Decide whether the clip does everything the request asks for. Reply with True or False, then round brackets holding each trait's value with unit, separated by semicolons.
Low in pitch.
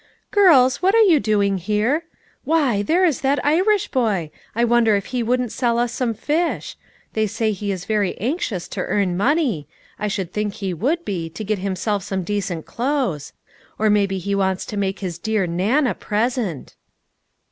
False (215 Hz)